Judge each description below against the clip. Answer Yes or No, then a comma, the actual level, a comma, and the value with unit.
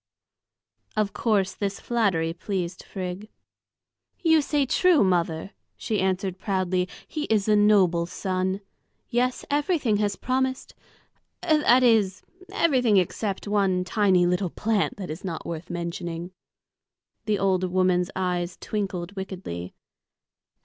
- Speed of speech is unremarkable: No, slow, 120 wpm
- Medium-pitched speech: No, high, 195 Hz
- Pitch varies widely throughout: No, average, 3.2 semitones